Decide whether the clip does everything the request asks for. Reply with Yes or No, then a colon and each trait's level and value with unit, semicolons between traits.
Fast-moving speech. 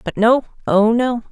No: slow, 135 wpm